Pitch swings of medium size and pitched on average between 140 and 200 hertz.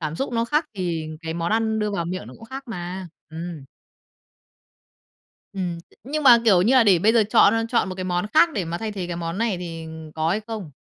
Yes: average, 5.0 semitones; high, 190 Hz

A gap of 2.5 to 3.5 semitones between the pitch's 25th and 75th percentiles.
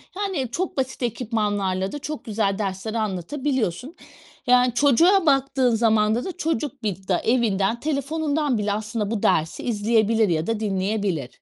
No: average, 5.0 semitones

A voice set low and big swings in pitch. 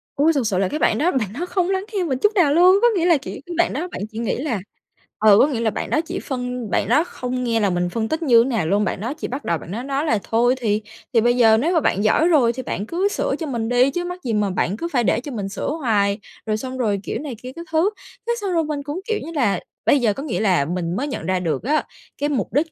No: very high, 255 Hz; wide, 6.4 semitones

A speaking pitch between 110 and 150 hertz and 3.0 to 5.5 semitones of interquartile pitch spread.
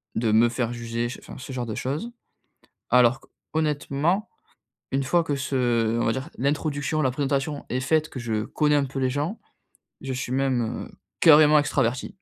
Yes: low, 135 Hz; average, 3.4 semitones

